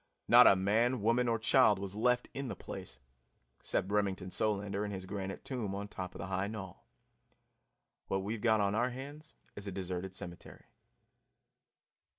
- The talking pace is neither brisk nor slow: Yes, average, 165 wpm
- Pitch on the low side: Yes, low, 100 Hz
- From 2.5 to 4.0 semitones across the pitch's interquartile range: Yes, average, 3.2 semitones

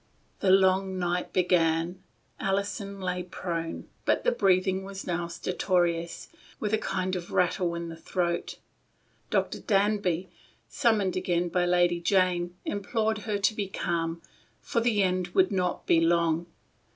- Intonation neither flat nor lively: No, narrow, 2.1 semitones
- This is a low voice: No, medium, 185 Hz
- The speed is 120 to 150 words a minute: Yes, average, 145 wpm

